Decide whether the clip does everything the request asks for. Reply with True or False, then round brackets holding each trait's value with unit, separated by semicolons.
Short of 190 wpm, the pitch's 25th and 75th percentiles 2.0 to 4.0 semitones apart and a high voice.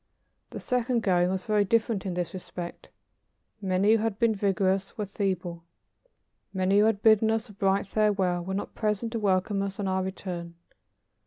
True (175 wpm; 2.4 semitones; 195 Hz)